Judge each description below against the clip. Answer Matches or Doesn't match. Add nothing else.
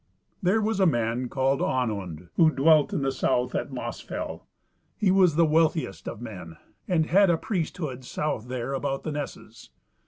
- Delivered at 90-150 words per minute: Doesn't match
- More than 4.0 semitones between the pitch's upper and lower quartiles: Matches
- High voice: Doesn't match